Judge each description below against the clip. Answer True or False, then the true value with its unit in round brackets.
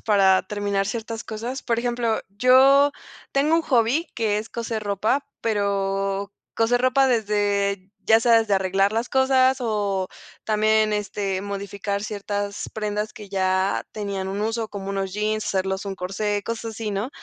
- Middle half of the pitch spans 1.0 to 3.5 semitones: True (2.5 semitones)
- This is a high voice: True (210 Hz)